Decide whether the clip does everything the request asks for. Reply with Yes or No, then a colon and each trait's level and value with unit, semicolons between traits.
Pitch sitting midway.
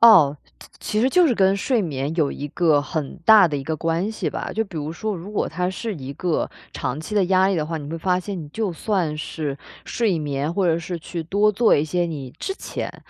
Yes: medium, 170 Hz